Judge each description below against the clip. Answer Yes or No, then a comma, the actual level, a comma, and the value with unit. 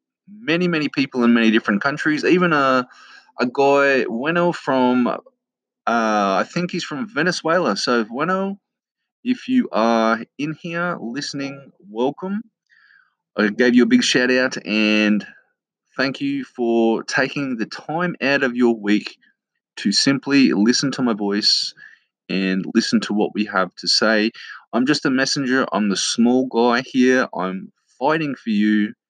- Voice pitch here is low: Yes, low, 130 Hz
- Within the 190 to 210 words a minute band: No, average, 150 wpm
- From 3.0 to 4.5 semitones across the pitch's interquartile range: No, wide, 5.4 semitones